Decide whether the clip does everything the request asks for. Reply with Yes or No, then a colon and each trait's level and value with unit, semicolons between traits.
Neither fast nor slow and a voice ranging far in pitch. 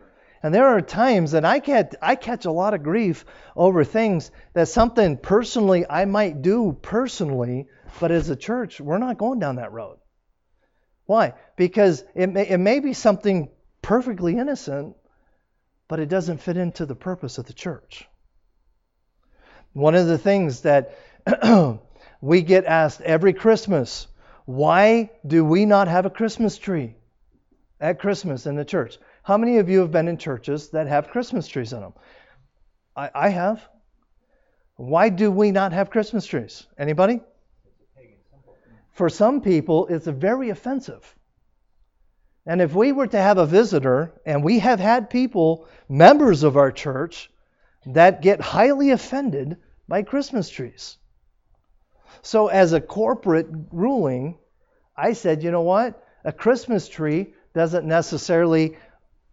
Yes: average, 150 wpm; wide, 6.0 semitones